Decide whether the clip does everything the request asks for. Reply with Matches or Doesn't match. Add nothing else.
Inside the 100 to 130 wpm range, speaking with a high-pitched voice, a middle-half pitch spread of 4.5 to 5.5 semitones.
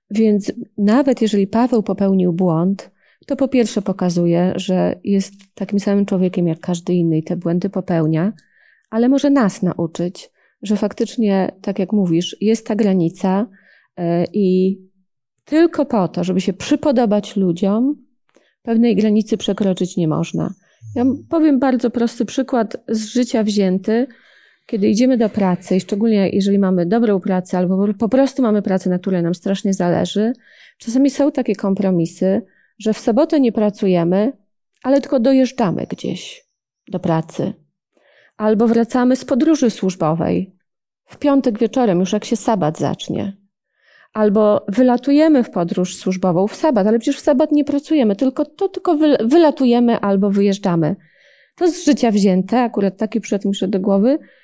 Doesn't match